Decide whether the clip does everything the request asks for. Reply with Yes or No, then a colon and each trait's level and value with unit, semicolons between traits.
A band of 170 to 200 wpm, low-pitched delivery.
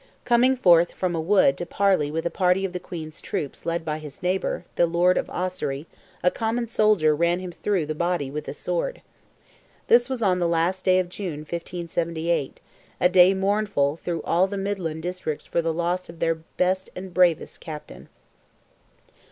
No: average, 180 wpm; medium, 175 Hz